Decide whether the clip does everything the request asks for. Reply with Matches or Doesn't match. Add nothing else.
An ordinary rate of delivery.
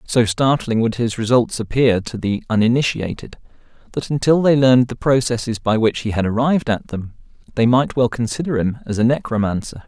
Matches